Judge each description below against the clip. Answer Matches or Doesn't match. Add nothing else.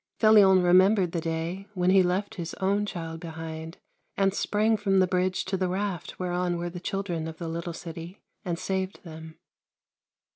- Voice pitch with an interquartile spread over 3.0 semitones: Doesn't match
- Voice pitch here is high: Doesn't match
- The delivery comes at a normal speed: Matches